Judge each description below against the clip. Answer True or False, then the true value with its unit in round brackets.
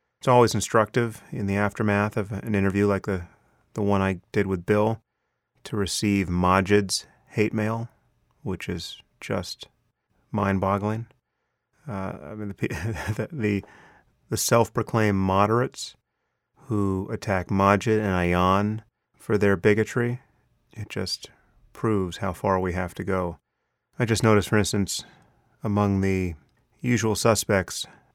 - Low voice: True (105 Hz)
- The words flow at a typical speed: False (130 wpm)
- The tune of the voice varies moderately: False (2.3 semitones)